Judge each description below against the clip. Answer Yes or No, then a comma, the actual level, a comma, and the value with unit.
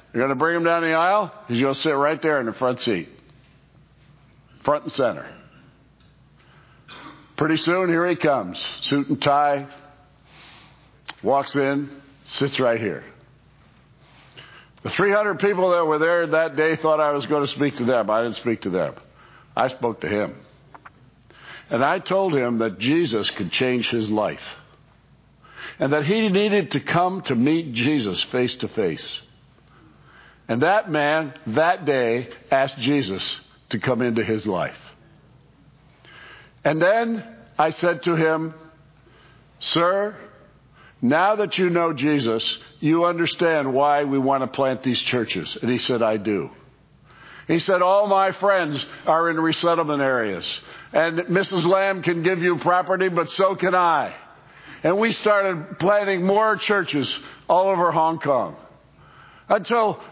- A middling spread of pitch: Yes, average, 4.6 semitones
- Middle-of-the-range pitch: Yes, medium, 155 Hz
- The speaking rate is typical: Yes, average, 150 wpm